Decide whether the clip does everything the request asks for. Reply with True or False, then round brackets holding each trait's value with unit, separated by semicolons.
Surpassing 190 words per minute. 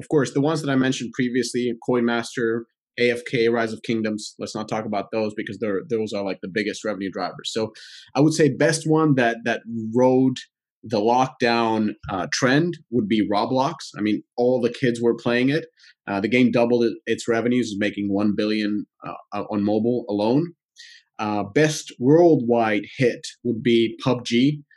False (175 wpm)